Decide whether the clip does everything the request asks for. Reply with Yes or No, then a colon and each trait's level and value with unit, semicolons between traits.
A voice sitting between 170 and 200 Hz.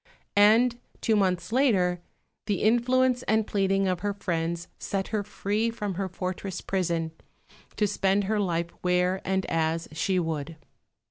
Yes: high, 190 Hz